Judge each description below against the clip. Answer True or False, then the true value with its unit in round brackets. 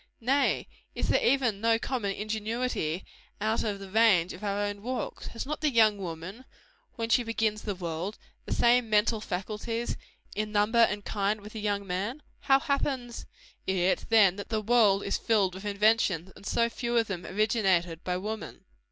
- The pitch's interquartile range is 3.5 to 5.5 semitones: False (2.8 semitones)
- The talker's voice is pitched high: True (215 Hz)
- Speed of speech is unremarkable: True (180 wpm)